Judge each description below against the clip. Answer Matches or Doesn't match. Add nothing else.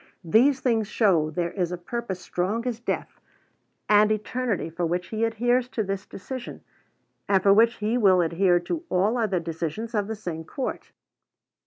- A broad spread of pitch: Doesn't match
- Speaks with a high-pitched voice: Matches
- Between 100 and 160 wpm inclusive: Doesn't match